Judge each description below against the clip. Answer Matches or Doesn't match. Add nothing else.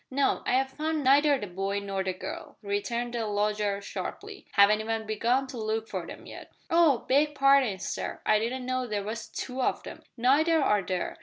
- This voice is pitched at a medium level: Doesn't match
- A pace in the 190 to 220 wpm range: Matches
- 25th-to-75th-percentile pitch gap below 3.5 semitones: Doesn't match